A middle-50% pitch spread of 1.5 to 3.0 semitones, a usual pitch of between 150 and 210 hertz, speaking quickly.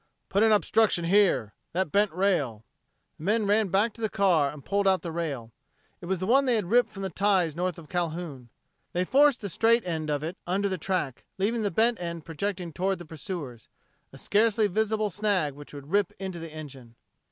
No: average, 4.4 semitones; medium, 185 Hz; fast, 210 wpm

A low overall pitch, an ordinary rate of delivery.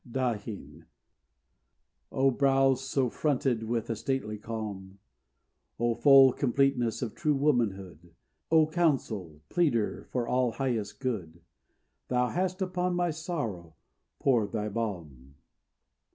No: low, 120 Hz; slow, 110 wpm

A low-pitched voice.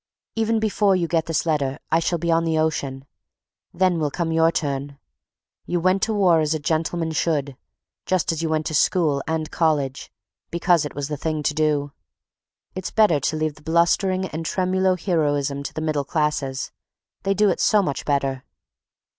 No: medium, 160 Hz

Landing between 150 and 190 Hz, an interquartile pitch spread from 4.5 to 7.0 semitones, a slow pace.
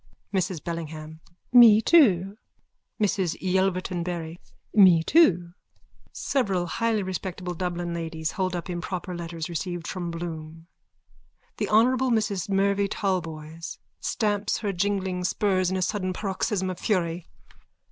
No: medium, 185 Hz; average, 2.8 semitones; slow, 120 wpm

